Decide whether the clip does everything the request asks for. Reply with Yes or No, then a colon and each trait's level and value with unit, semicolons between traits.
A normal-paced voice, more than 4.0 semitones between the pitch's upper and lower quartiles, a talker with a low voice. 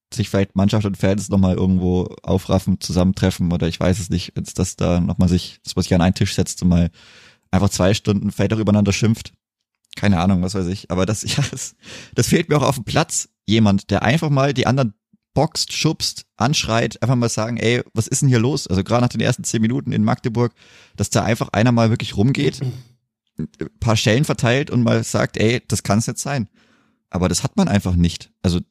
No: fast, 220 wpm; average, 4.5 semitones; low, 105 Hz